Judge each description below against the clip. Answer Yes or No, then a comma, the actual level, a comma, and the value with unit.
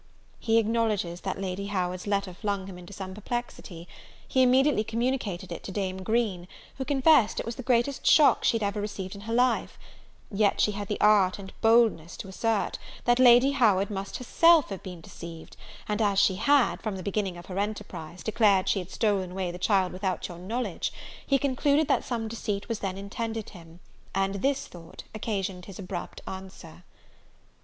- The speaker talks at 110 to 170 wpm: No, average, 185 wpm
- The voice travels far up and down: No, average, 3.6 semitones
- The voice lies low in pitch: No, high, 205 Hz